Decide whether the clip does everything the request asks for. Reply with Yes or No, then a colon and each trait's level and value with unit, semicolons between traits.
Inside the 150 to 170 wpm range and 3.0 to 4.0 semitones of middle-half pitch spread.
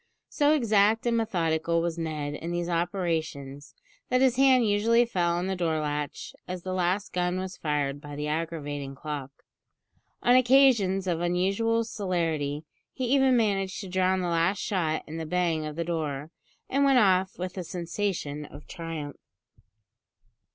No: average, 160 wpm; average, 4.5 semitones